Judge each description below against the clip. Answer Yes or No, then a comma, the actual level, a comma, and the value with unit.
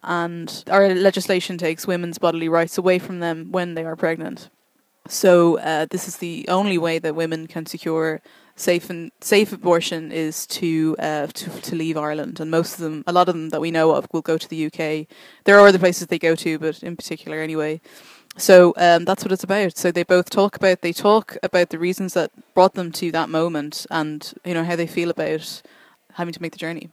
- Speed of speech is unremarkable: No, fast, 220 wpm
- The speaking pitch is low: No, medium, 170 Hz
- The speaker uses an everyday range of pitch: No, narrow, 2.2 semitones